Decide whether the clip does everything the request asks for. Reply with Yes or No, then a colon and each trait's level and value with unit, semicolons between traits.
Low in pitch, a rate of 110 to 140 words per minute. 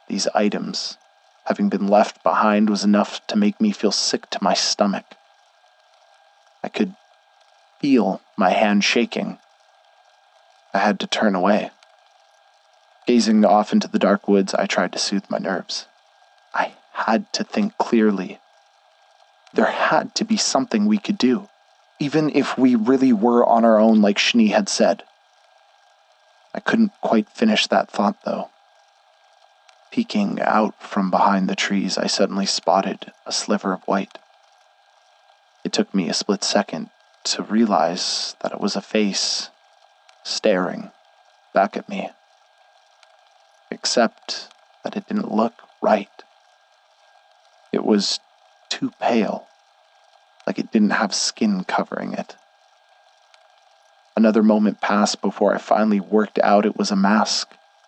Yes: low, 120 Hz; slow, 135 wpm